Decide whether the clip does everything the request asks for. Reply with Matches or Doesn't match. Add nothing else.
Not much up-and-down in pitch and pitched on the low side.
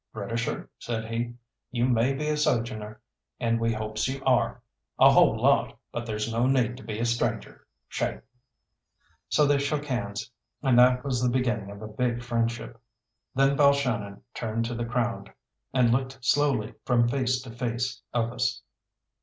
Matches